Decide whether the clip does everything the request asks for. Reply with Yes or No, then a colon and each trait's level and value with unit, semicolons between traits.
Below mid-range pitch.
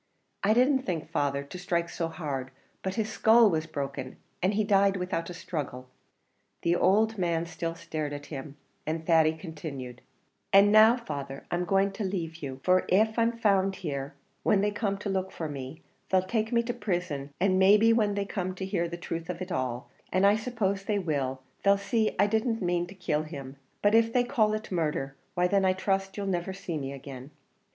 No: medium, 185 Hz